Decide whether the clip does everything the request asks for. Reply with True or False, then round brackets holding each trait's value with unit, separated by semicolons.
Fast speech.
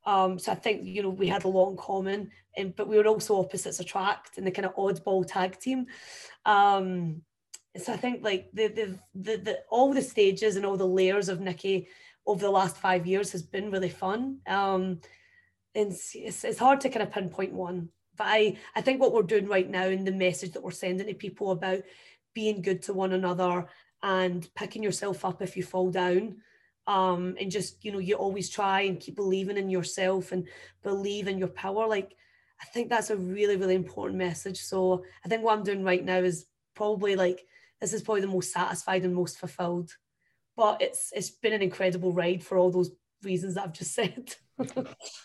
True (210 wpm)